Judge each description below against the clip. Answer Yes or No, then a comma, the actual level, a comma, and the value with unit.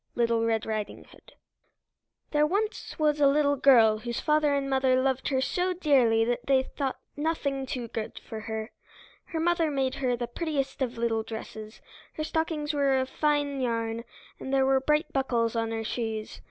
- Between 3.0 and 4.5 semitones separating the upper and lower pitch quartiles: Yes, average, 4.2 semitones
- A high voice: Yes, very high, 265 Hz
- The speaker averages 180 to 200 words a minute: Yes, average, 185 wpm